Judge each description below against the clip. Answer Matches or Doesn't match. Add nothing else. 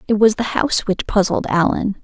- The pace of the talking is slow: Doesn't match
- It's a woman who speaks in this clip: Matches